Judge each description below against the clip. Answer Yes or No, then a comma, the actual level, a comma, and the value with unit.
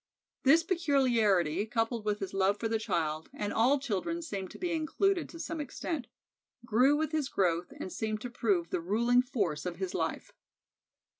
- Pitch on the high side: Yes, high, 225 Hz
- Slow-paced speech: No, average, 175 wpm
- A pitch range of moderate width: No, wide, 6.8 semitones